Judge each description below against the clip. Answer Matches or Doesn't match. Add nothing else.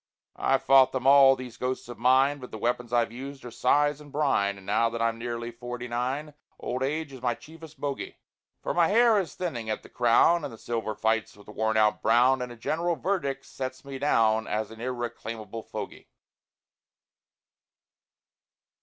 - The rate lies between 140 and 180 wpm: Doesn't match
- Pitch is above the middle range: Doesn't match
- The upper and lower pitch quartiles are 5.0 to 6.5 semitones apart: Doesn't match